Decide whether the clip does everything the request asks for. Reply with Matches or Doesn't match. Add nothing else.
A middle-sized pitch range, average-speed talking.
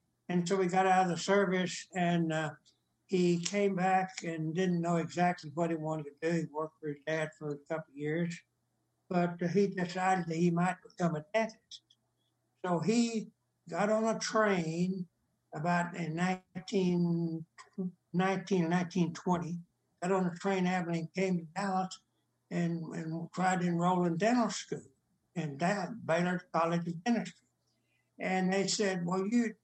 Doesn't match